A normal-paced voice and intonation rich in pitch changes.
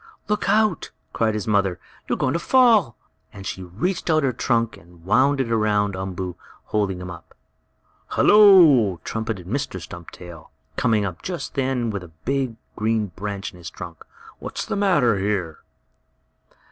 Yes: average, 160 wpm; wide, 6.4 semitones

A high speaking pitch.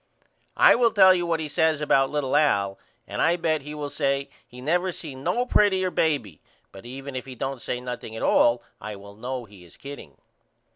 No: medium, 140 Hz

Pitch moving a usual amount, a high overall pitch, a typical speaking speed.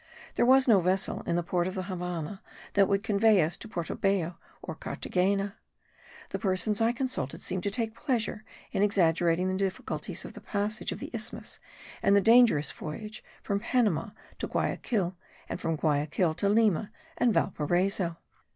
Yes: average, 3.6 semitones; high, 195 Hz; average, 170 wpm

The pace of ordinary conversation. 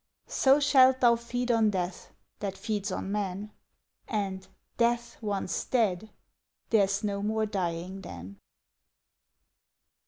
No: slow, 115 wpm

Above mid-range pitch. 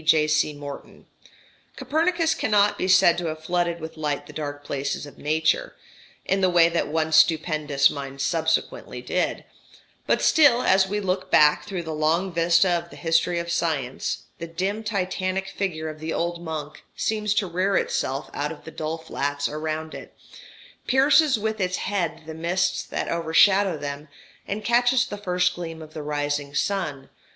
No: medium, 170 Hz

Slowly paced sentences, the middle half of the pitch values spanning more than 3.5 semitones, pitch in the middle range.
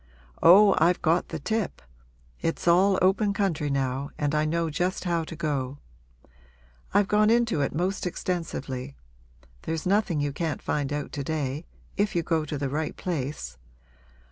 No: average, 160 wpm; average, 4.2 semitones; medium, 160 Hz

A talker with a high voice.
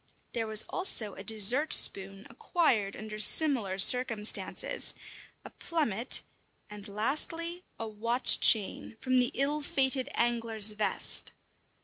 Yes: high, 230 Hz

